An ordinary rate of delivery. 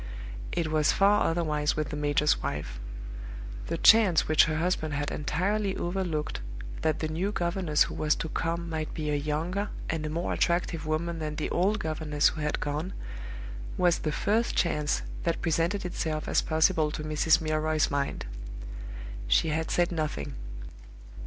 Yes: average, 160 wpm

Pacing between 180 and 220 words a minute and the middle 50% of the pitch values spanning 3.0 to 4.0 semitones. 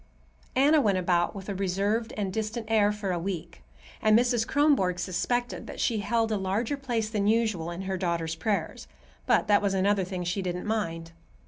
Yes: average, 190 wpm; average, 3.4 semitones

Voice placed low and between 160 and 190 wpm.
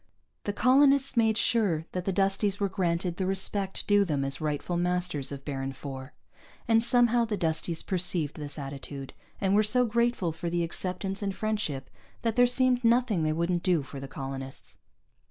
No: medium, 185 Hz; average, 175 wpm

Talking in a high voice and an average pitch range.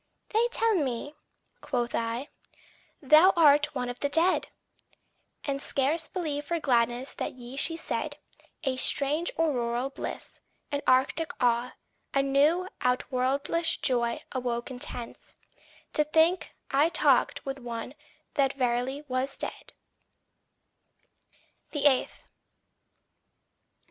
Yes: very high, 275 Hz; average, 3.6 semitones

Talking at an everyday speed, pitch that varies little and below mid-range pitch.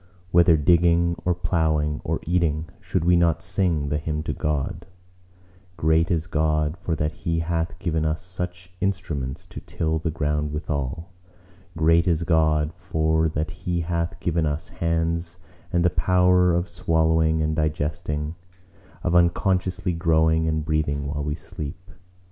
Yes: average, 150 wpm; narrow, 2.0 semitones; very low, 80 Hz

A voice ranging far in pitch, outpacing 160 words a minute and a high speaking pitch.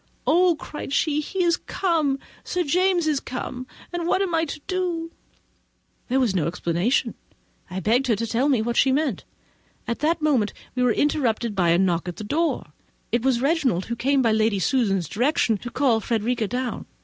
Yes: wide, 6.0 semitones; average, 185 wpm; very high, 255 Hz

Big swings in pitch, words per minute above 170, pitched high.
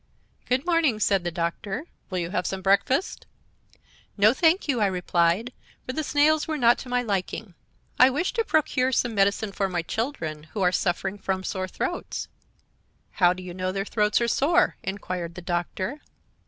Yes: wide, 6.0 semitones; average, 180 wpm; high, 205 Hz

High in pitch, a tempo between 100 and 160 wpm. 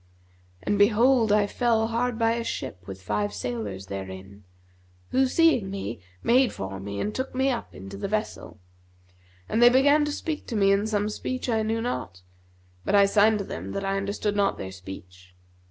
No: high, 205 Hz; average, 185 wpm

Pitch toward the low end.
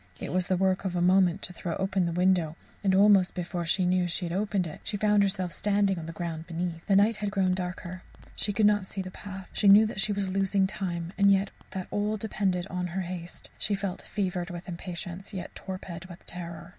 No: medium, 185 Hz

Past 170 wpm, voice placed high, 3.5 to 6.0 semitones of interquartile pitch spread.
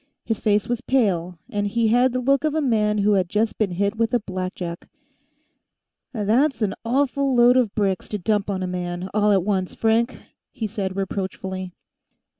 Yes: average, 185 wpm; high, 210 Hz; average, 3.9 semitones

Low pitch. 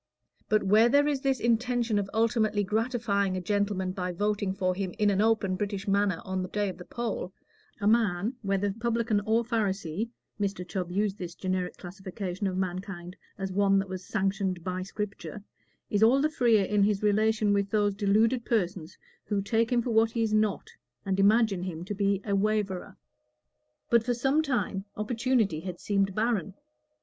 No: high, 205 Hz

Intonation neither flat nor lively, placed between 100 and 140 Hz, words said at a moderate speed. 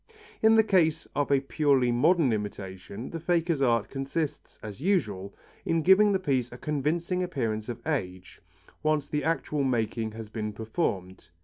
No: wide, 7.0 semitones; low, 135 Hz; average, 155 wpm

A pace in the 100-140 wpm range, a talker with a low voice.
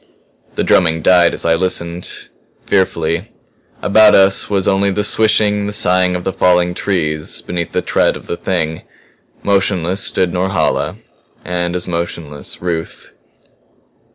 Yes: slow, 135 wpm; very low, 90 Hz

